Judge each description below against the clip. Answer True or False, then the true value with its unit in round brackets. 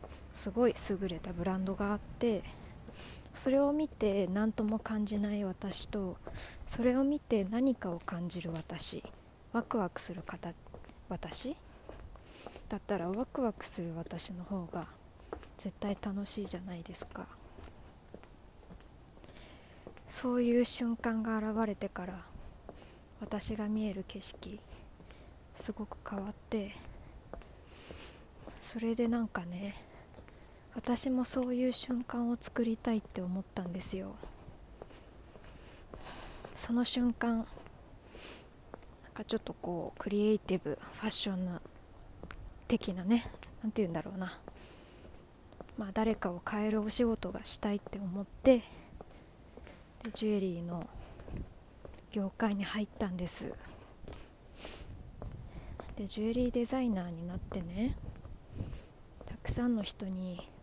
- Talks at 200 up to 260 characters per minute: True (225 characters per minute)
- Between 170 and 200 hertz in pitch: False (210 Hz)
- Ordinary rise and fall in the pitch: True (3.9 semitones)